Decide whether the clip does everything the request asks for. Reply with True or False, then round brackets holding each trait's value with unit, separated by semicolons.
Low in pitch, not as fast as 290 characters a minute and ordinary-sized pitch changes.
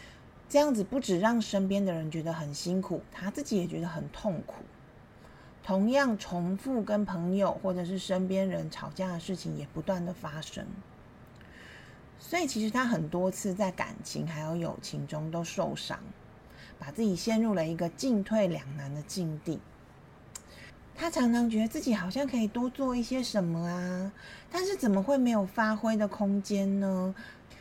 False (195 Hz; 245 characters per minute; 4.3 semitones)